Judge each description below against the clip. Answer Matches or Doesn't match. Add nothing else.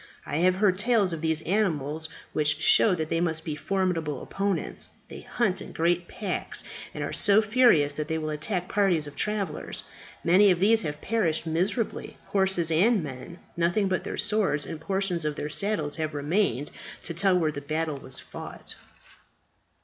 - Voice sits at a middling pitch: Matches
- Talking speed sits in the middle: Matches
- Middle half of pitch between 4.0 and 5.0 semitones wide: Matches